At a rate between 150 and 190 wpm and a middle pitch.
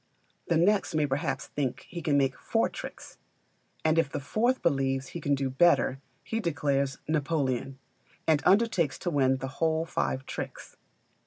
Yes: average, 160 wpm; medium, 145 Hz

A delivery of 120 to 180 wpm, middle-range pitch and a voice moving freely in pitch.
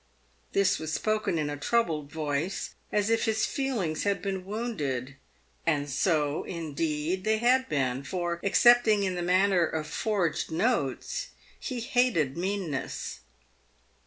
Yes: slow, 135 wpm; medium, 180 Hz; wide, 6.0 semitones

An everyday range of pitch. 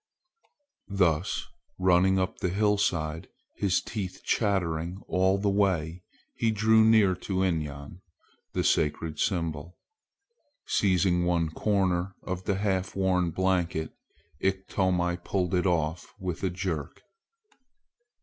No: narrow, 2.3 semitones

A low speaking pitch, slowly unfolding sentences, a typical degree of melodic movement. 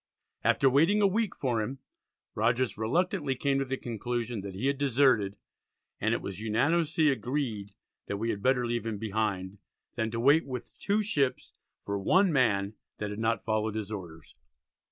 No: low, 120 Hz; average, 175 wpm; average, 4.6 semitones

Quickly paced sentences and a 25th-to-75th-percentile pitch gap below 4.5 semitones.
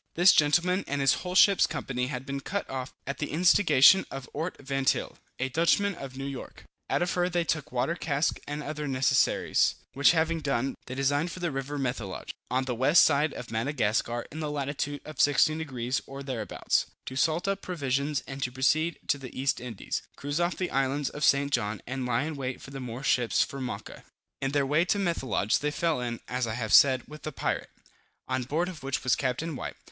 Yes: fast, 210 wpm; average, 3.4 semitones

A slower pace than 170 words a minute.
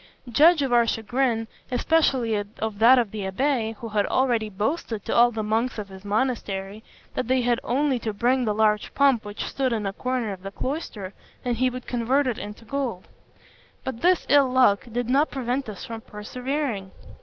No: average, 190 wpm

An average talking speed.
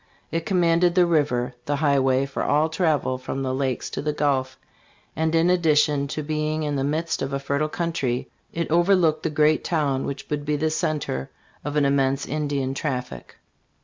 Yes: average, 185 wpm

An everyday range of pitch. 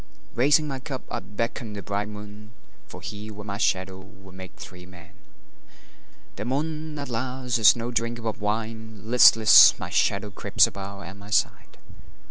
Yes: average, 3.3 semitones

